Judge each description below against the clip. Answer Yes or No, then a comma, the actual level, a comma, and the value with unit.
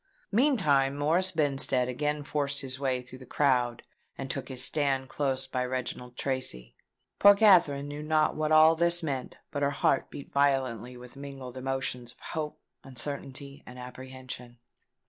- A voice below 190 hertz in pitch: Yes, low, 135 Hz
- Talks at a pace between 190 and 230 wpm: No, average, 155 wpm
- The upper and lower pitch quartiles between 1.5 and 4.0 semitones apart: Yes, narrow, 2.6 semitones